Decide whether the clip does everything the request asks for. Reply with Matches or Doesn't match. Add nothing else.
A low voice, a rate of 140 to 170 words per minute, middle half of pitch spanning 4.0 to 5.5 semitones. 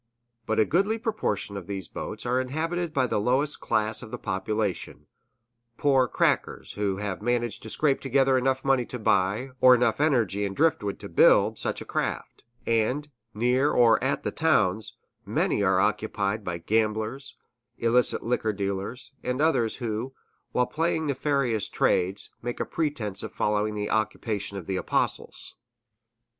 Matches